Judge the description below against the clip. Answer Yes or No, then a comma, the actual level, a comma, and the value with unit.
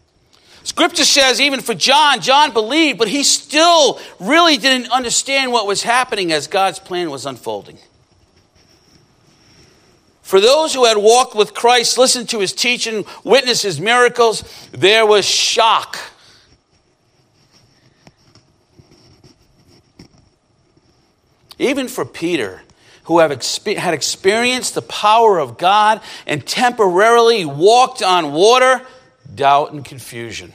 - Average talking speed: No, slow, 110 wpm